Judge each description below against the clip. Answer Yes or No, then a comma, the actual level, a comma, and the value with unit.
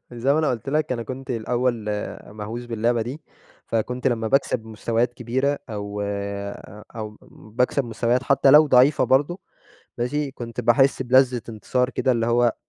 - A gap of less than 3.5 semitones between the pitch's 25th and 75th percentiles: Yes, average, 2.7 semitones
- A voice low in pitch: Yes, low, 120 Hz